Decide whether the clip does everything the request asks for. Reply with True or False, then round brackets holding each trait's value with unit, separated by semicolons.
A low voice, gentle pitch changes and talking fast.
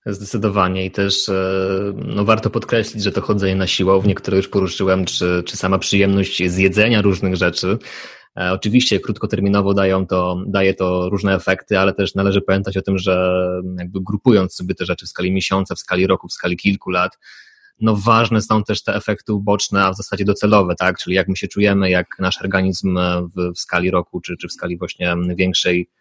True (95 Hz; 1.6 semitones; 185 wpm)